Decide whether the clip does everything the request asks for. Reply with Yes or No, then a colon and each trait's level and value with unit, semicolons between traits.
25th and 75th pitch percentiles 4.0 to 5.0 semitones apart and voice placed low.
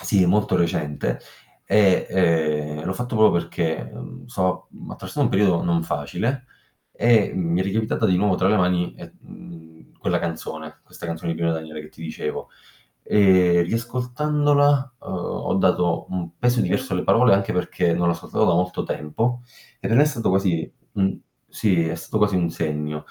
Yes: average, 4.5 semitones; very low, 90 Hz